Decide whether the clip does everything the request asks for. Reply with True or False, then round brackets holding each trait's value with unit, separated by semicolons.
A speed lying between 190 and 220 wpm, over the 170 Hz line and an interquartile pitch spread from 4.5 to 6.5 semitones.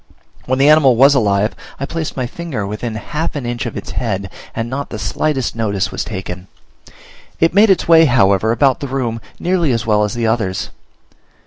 False (195 wpm; 120 Hz; 5.1 semitones)